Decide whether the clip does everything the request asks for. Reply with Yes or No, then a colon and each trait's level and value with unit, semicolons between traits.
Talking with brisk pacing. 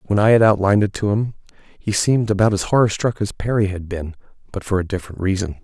Yes: fast, 235 wpm